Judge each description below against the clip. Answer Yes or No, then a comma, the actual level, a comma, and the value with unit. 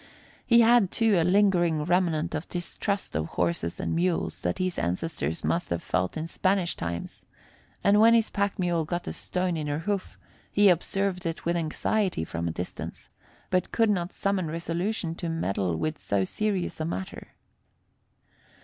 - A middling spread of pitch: Yes, average, 4.2 semitones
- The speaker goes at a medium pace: Yes, average, 170 wpm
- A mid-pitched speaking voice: Yes, medium, 175 Hz